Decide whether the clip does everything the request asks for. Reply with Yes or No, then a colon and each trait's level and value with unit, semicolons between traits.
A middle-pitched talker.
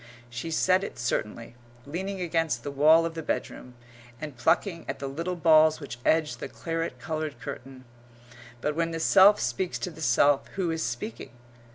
Yes: medium, 155 Hz